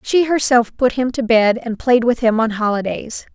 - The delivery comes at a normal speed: No, fast, 215 wpm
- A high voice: Yes, high, 235 Hz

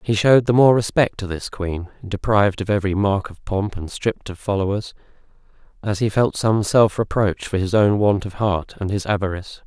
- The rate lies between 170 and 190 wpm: No, fast, 205 wpm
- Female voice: No, male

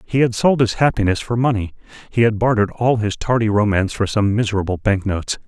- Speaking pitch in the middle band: No, low, 110 Hz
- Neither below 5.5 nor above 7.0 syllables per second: Yes, 6.3 syllables/s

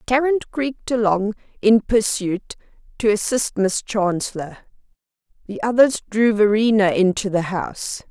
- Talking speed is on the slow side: Yes, slow, 120 wpm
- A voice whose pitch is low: No, high, 215 Hz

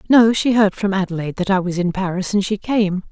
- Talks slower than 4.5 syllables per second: No, 5.9 syllables/s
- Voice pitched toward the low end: No, high, 195 Hz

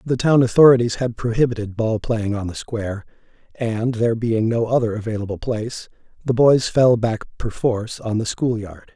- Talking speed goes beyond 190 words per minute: No, average, 175 wpm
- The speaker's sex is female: No, male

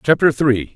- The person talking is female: No, male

